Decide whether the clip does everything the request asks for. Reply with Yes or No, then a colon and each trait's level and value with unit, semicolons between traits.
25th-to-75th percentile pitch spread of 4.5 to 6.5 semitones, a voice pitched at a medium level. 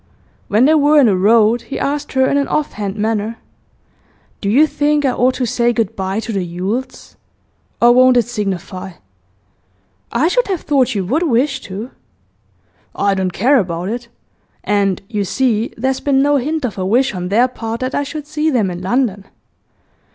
No: average, 5.2 semitones; high, 235 Hz